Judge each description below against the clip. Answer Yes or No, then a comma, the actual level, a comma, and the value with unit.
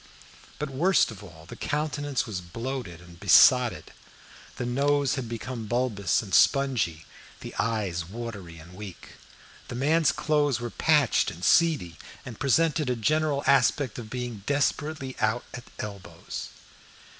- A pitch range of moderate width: No, wide, 5.8 semitones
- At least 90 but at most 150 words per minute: Yes, average, 140 wpm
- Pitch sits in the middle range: No, low, 120 Hz